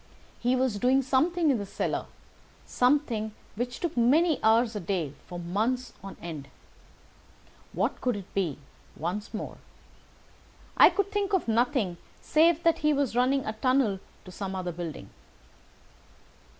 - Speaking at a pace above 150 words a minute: No, average, 140 wpm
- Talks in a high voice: Yes, high, 240 Hz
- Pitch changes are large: Yes, wide, 5.9 semitones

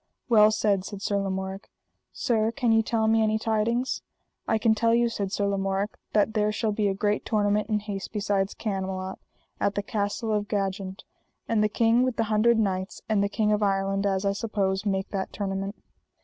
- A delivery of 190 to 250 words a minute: Yes, average, 195 wpm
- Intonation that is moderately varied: No, narrow, 1.9 semitones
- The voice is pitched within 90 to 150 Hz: No, high, 210 Hz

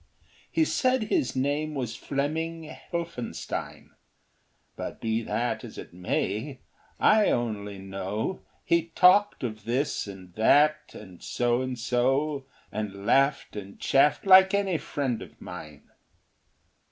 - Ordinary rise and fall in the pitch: No, wide, 6.8 semitones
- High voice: No, low, 130 Hz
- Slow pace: Yes, slow, 125 wpm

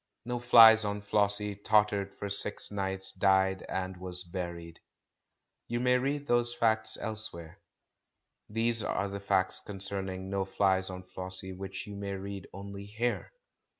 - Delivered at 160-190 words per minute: No, average, 140 wpm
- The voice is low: Yes, low, 100 Hz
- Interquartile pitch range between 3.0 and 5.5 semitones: No, narrow, 2.4 semitones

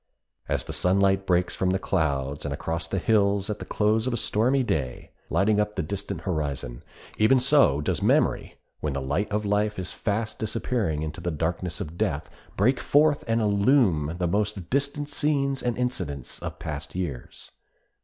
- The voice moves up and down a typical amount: No, wide, 5.8 semitones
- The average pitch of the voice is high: No, low, 100 Hz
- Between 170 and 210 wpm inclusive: Yes, average, 175 wpm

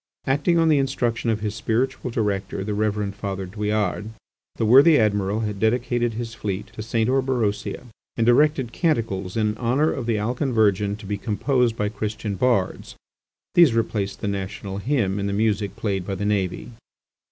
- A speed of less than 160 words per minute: No, average, 170 wpm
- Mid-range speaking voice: No, low, 110 Hz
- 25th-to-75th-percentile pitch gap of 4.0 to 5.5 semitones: No, average, 3.1 semitones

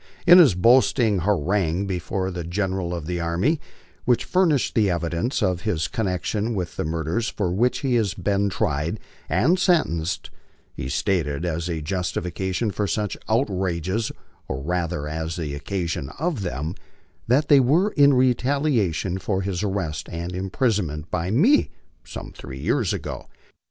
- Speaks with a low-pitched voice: Yes, very low, 95 Hz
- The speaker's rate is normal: Yes, average, 155 wpm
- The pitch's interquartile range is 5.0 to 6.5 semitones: Yes, wide, 5.5 semitones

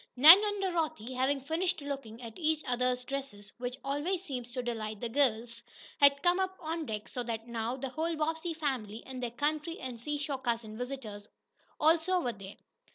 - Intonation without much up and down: No, average, 5.1 semitones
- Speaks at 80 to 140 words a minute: No, average, 175 wpm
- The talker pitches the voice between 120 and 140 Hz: No, very high, 270 Hz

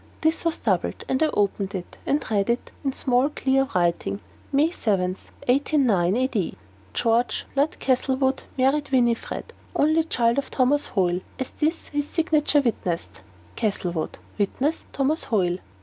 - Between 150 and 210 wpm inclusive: No, slow, 135 wpm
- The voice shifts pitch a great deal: Yes, wide, 6.5 semitones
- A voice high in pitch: Yes, very high, 255 Hz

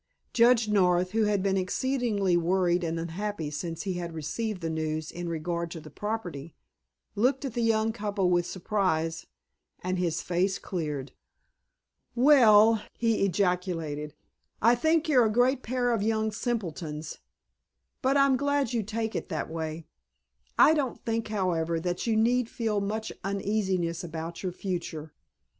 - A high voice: Yes, high, 195 Hz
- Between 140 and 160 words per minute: Yes, average, 150 wpm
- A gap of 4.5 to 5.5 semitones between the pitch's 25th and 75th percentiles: Yes, average, 5.0 semitones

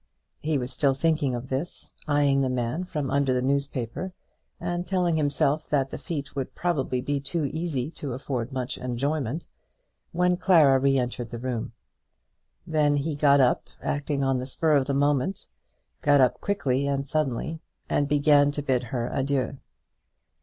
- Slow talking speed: No, average, 165 wpm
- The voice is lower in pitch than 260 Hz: Yes, medium, 140 Hz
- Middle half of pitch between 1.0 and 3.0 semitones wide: Yes, narrow, 2.6 semitones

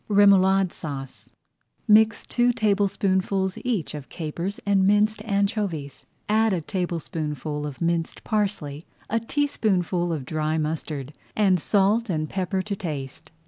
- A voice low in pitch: No, high, 190 Hz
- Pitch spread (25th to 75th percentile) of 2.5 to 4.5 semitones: No, average, 4.9 semitones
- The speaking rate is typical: No, slow, 125 wpm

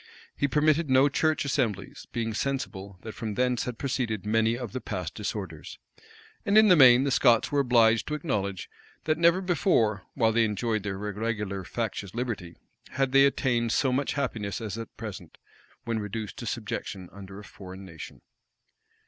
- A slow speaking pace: No, average, 170 wpm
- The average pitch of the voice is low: Yes, low, 115 Hz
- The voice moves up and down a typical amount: Yes, average, 4.7 semitones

